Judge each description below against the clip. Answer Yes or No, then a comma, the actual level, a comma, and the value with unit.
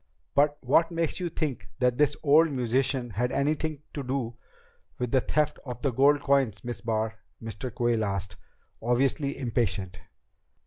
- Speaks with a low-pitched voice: Yes, low, 130 Hz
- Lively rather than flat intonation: No, average, 3.7 semitones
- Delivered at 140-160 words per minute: Yes, average, 145 wpm